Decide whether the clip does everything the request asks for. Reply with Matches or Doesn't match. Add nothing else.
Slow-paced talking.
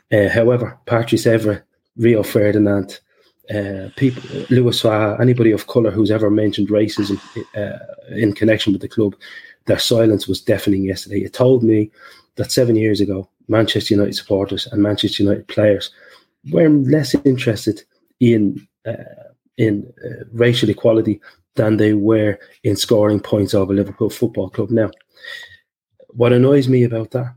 Doesn't match